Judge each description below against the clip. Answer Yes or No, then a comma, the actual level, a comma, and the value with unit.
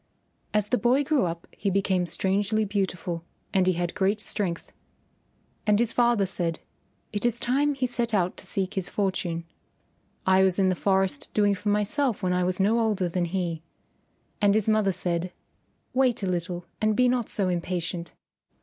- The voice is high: Yes, high, 195 Hz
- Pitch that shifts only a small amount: No, average, 3.2 semitones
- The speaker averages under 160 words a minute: No, average, 175 wpm